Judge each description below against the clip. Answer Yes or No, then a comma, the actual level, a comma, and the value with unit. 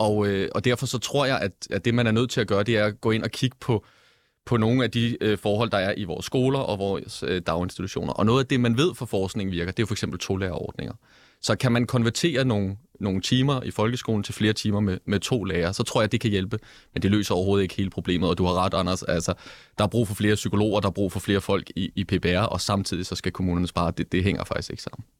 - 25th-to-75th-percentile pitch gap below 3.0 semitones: No, average, 3.7 semitones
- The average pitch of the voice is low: Yes, low, 105 Hz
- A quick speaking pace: Yes, fast, 270 wpm